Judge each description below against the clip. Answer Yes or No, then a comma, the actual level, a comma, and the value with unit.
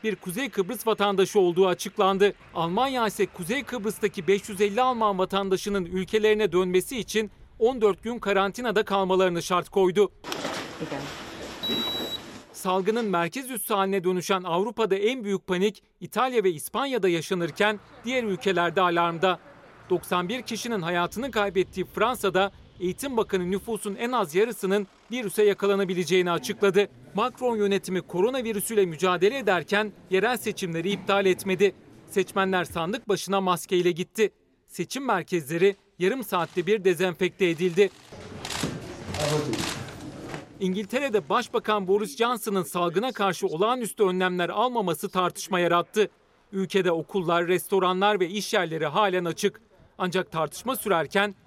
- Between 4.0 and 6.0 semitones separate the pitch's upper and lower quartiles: No, average, 2.7 semitones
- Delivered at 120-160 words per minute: No, average, 110 wpm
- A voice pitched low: No, high, 195 Hz